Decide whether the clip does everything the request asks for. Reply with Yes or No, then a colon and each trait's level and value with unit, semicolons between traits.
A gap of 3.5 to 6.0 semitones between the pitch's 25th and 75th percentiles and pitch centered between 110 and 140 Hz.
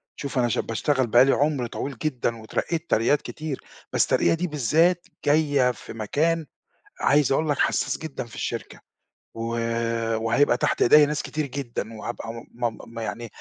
Yes: average, 4.4 semitones; low, 135 Hz